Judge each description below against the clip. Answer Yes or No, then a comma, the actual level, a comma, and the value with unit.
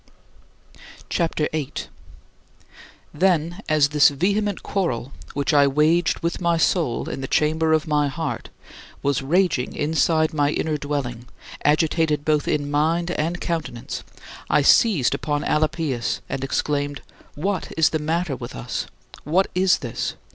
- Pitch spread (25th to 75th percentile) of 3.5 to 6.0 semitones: No, average, 2.7 semitones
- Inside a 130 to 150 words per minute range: Yes, average, 140 wpm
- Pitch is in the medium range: Yes, medium, 155 Hz